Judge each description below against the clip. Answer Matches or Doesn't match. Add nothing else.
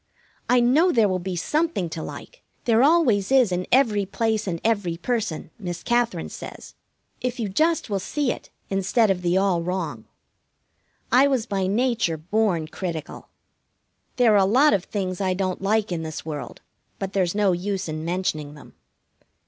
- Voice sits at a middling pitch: Doesn't match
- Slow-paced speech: Doesn't match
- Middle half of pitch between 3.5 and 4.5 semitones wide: Doesn't match